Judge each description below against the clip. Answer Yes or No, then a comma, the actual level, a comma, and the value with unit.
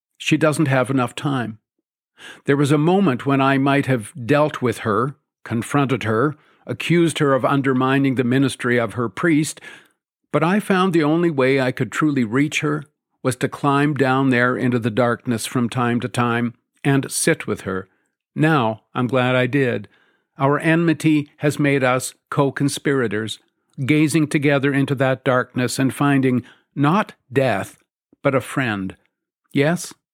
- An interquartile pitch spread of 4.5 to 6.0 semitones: No, average, 3.2 semitones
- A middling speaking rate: Yes, average, 155 wpm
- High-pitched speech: No, low, 135 Hz